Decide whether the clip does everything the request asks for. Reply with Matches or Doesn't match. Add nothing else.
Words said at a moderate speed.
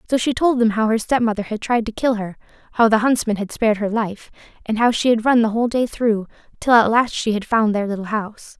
Doesn't match